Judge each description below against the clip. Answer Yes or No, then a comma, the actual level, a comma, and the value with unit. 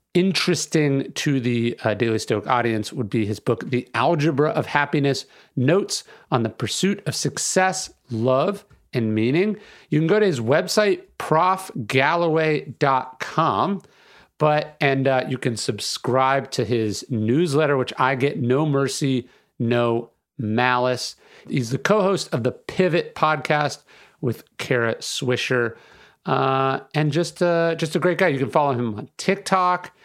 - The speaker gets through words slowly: No, average, 145 wpm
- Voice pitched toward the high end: No, medium, 140 Hz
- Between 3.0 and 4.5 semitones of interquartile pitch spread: No, average, 5.3 semitones